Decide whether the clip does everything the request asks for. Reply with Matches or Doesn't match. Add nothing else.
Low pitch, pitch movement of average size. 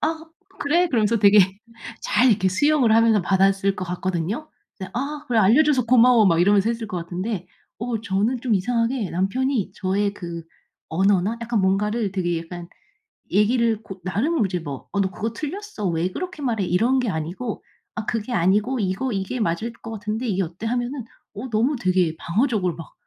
Doesn't match